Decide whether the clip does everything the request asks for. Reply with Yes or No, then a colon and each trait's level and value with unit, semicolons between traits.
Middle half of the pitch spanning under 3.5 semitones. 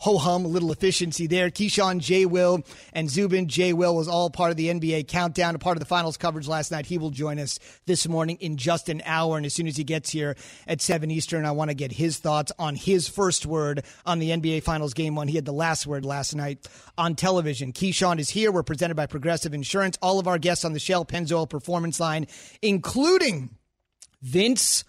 Yes: narrow, 2.5 semitones